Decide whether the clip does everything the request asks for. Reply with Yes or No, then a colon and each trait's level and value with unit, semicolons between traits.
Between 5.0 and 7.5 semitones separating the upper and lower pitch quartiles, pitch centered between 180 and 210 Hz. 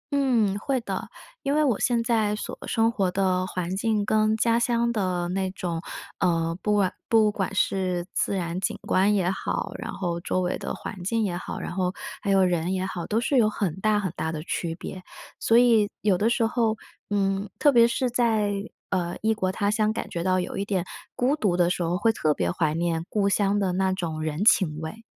No: average, 3.7 semitones; high, 195 Hz